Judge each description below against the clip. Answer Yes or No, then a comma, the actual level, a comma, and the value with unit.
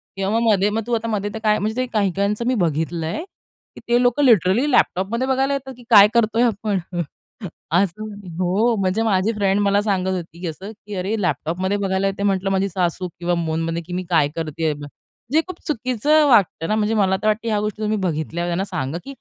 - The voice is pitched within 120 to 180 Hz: No, high, 200 Hz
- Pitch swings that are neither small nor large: Yes, average, 3.7 semitones